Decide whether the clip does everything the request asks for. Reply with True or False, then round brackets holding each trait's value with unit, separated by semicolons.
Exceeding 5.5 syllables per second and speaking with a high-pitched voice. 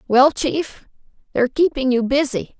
False (4.6 syllables/s; 260 Hz)